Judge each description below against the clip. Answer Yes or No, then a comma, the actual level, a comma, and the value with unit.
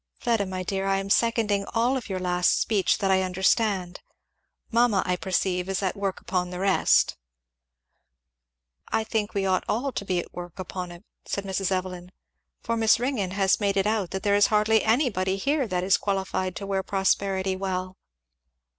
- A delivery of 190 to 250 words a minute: No, average, 180 wpm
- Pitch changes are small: Yes, narrow, 2.2 semitones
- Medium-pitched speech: No, high, 195 Hz